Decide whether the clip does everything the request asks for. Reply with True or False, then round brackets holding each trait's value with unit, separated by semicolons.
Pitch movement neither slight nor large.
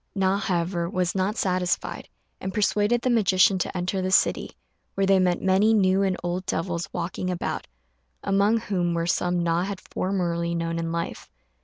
False (2.0 semitones)